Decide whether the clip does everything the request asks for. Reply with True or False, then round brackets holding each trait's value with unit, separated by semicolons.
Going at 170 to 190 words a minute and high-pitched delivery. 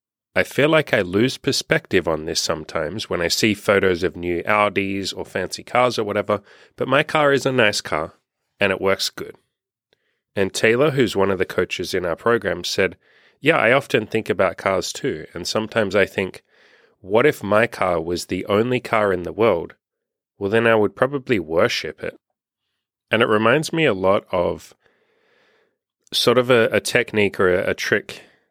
False (185 wpm; 110 Hz)